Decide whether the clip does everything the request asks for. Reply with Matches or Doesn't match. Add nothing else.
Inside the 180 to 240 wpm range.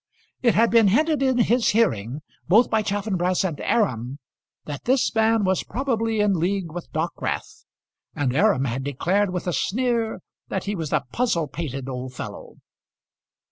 Doesn't match